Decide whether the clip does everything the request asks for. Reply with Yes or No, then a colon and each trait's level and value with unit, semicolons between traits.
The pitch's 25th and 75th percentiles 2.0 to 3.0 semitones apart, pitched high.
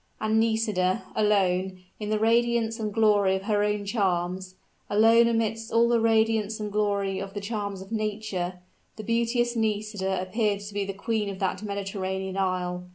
Yes: narrow, 2.6 semitones; high, 210 Hz